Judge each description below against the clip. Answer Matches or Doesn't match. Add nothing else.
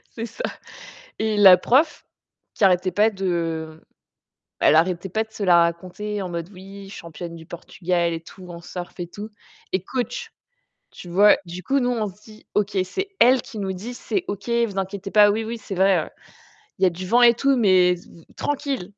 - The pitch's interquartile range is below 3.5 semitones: Doesn't match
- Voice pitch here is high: Matches